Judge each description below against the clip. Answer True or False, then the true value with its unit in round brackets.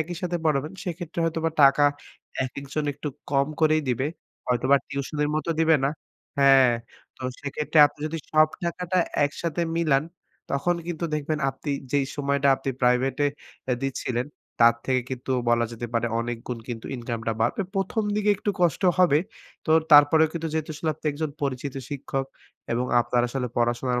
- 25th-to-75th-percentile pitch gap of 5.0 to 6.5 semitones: False (3.7 semitones)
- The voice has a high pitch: False (140 Hz)